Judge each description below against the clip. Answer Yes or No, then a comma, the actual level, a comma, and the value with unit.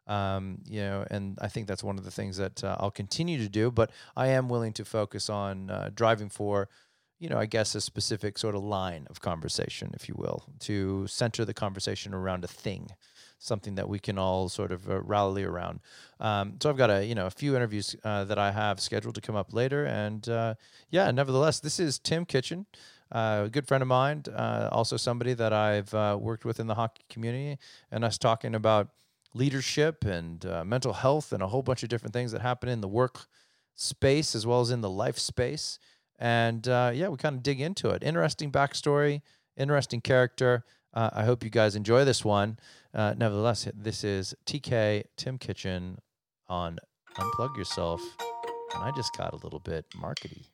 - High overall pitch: No, low, 115 Hz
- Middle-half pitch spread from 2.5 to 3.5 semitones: No, average, 4.1 semitones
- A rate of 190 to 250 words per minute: Yes, average, 200 wpm